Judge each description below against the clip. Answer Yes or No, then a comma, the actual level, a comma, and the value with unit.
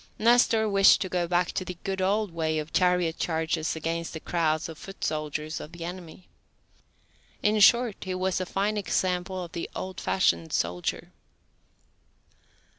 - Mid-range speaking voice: Yes, medium, 180 Hz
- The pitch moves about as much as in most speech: Yes, average, 3.1 semitones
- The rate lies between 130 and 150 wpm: No, average, 160 wpm